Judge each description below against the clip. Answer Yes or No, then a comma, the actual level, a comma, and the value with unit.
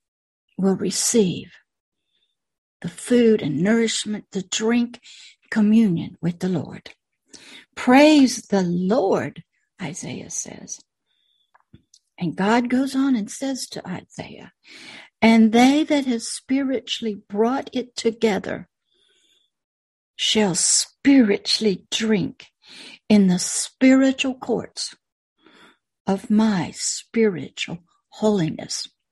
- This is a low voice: No, high, 225 Hz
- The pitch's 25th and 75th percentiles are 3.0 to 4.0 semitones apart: No, average, 4.4 semitones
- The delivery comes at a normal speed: No, slow, 90 wpm